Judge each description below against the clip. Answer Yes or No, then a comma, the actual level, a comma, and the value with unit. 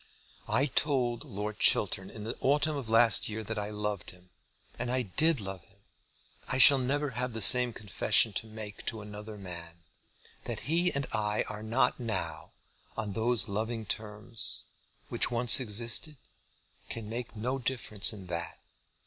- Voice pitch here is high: No, low, 110 Hz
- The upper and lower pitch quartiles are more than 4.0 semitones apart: No, average, 3.2 semitones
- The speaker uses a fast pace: No, average, 160 wpm